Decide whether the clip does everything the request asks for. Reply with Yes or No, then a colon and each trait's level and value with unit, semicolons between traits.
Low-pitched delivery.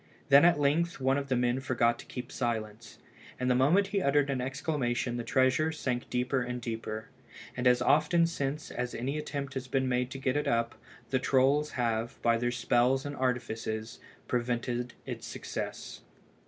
Yes: low, 130 Hz